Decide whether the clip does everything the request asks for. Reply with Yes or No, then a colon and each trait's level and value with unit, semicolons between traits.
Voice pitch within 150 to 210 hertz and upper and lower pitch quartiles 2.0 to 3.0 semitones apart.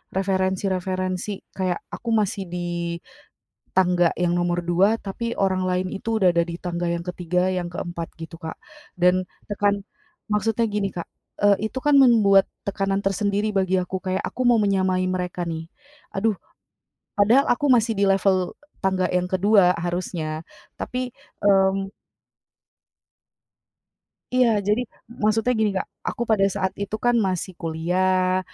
Yes: high, 190 Hz; narrow, 2.6 semitones